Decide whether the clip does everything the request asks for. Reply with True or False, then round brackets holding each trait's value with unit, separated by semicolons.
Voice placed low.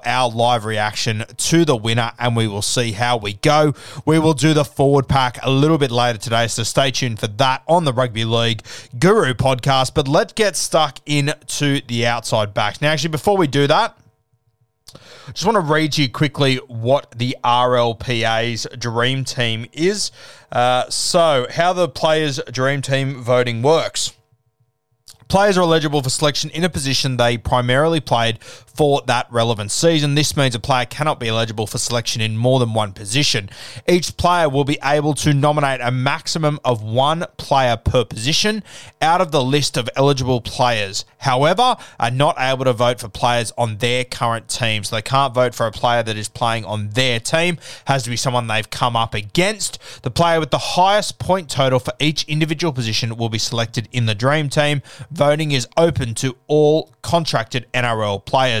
True (130 Hz)